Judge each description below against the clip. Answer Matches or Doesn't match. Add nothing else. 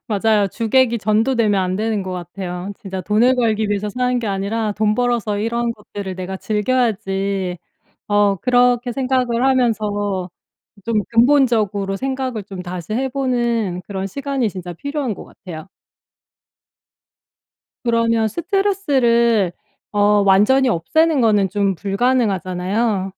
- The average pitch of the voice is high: Matches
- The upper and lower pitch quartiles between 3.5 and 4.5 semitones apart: Matches